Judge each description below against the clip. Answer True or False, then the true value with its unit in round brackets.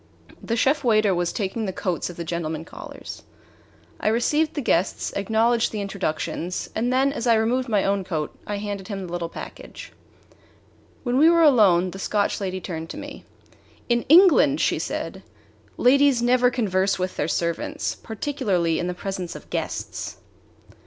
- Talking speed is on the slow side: False (165 wpm)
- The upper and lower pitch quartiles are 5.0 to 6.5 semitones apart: True (5.3 semitones)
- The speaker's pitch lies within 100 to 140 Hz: False (205 Hz)